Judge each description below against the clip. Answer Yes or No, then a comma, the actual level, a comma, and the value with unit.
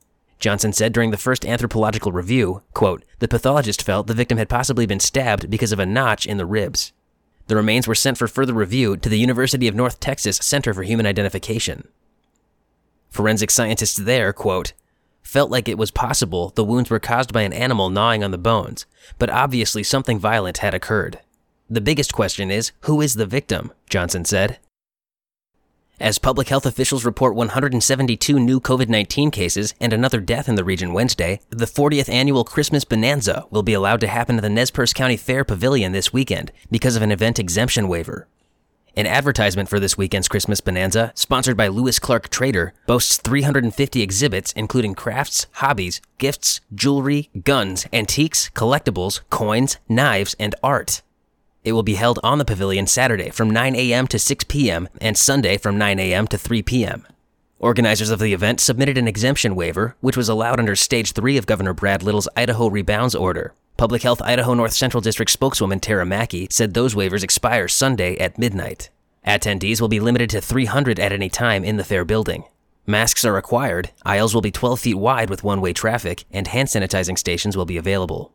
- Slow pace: No, average, 180 wpm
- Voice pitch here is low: Yes, low, 115 Hz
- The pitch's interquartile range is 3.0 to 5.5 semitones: Yes, average, 3.7 semitones